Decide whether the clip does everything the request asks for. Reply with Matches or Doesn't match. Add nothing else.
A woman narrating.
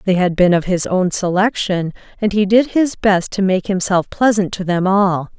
Matches